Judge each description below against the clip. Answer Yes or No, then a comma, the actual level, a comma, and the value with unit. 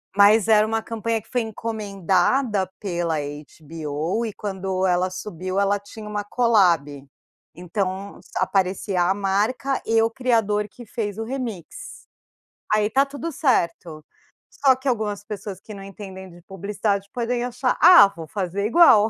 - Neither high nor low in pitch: No, high, 205 Hz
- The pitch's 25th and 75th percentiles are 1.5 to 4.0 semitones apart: Yes, average, 3.3 semitones